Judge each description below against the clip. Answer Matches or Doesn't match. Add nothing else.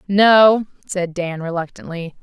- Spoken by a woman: Matches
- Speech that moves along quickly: Doesn't match